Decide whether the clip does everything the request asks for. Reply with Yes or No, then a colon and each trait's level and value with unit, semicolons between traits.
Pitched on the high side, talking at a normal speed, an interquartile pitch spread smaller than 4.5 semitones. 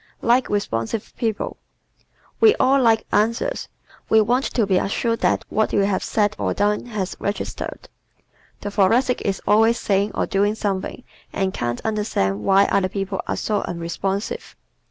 Yes: high, 205 Hz; average, 155 wpm; average, 2.7 semitones